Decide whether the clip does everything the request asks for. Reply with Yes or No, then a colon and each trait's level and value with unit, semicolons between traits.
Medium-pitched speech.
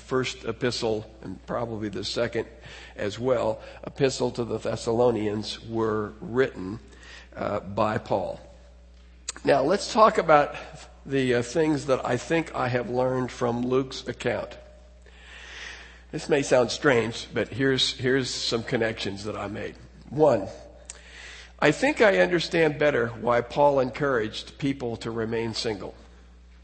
No: low, 115 Hz